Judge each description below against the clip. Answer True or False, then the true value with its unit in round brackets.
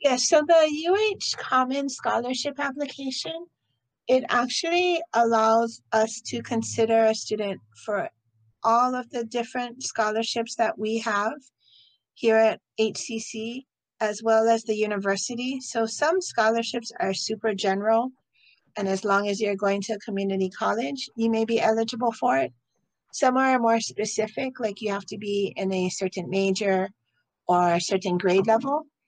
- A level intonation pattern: False (3.8 semitones)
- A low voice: False (225 Hz)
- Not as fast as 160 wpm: True (150 wpm)